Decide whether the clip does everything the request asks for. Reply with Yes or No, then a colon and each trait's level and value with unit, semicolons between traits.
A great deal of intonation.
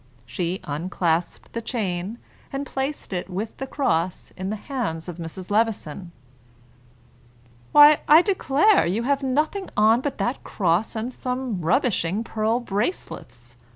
Yes: wide, 7.0 semitones